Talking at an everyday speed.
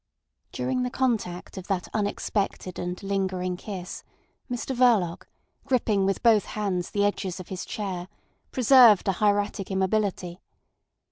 No: slow, 130 wpm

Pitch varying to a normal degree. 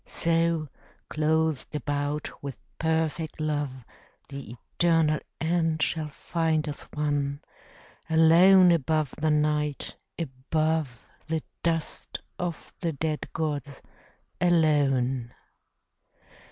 No: narrow, 2.0 semitones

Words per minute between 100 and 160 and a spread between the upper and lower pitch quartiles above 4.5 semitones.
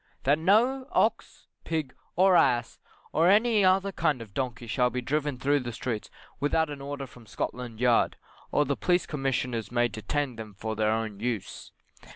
No: average, 175 wpm; average, 5.2 semitones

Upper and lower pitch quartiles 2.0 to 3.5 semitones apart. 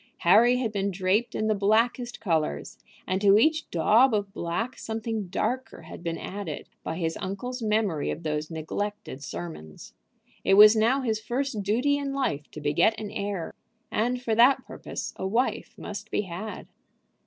No: average, 5.1 semitones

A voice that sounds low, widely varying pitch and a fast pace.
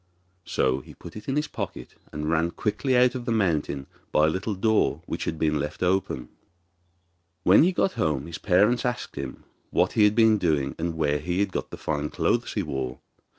Yes: very low, 90 Hz; wide, 6.4 semitones; fast, 210 wpm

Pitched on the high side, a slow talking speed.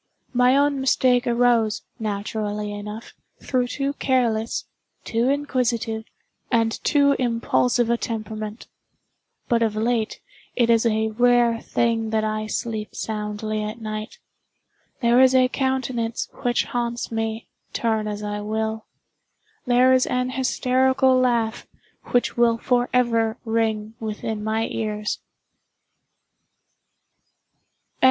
Yes: high, 230 Hz; slow, 115 wpm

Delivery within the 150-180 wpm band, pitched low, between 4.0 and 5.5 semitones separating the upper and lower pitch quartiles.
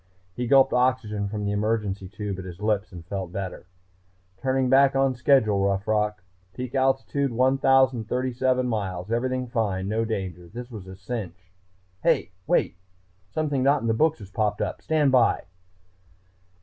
Yes: average, 160 wpm; low, 110 Hz; average, 4.6 semitones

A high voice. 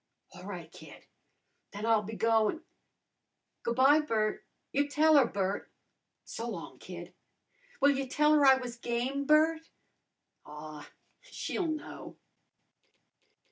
Yes: very high, 255 Hz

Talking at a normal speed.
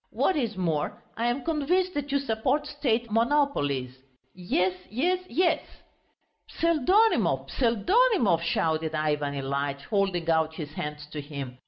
No: slow, 130 wpm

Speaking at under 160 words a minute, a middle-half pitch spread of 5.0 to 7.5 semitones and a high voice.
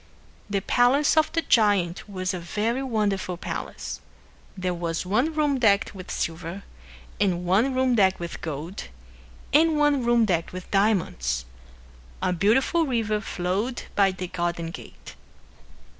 Yes: average, 140 wpm; wide, 5.4 semitones; high, 200 Hz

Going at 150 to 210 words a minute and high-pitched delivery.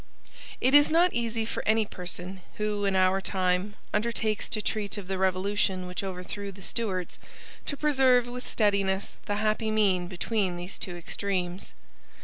Yes: average, 155 wpm; high, 200 Hz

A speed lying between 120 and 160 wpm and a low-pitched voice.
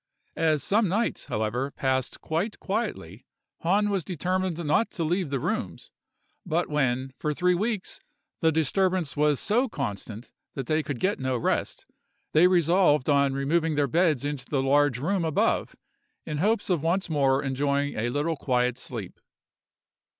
No: average, 155 wpm; medium, 150 Hz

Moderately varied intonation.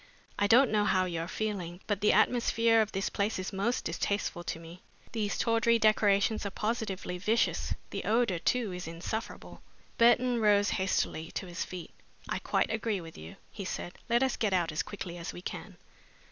Yes: average, 3.9 semitones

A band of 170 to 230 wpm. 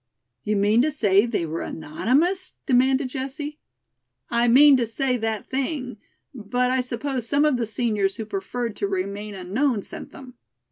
No: average, 160 wpm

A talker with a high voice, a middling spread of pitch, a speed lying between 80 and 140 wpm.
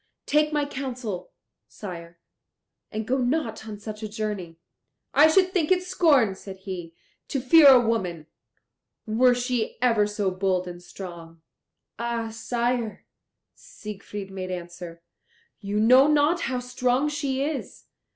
No: high, 225 Hz; wide, 5.7 semitones; slow, 135 wpm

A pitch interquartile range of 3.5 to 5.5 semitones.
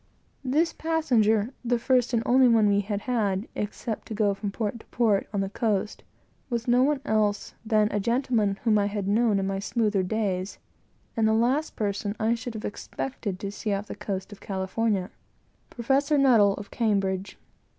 No: average, 2.9 semitones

